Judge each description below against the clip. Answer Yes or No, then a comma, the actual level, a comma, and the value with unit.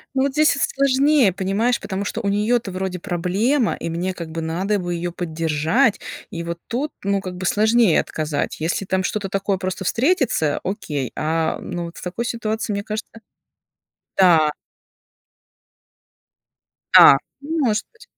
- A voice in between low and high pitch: No, high, 195 Hz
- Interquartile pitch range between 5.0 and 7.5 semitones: Yes, average, 5.3 semitones